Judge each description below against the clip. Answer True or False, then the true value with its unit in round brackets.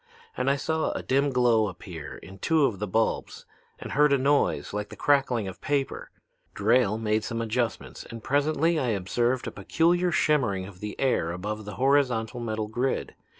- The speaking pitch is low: True (120 Hz)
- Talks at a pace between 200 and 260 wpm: False (180 wpm)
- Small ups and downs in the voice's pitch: False (4.8 semitones)